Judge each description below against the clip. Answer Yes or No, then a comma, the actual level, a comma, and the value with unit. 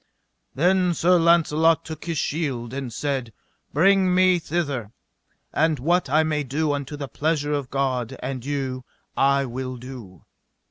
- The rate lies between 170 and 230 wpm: No, average, 145 wpm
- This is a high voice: No, medium, 145 Hz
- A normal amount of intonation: Yes, average, 4.0 semitones